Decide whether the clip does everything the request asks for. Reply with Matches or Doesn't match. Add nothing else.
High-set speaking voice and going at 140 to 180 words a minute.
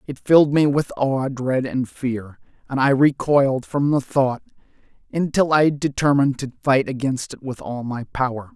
Doesn't match